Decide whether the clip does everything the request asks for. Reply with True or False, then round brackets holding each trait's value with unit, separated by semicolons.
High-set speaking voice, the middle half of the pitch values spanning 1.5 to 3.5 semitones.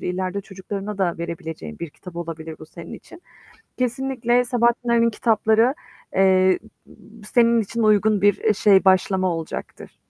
False (200 Hz; 4.4 semitones)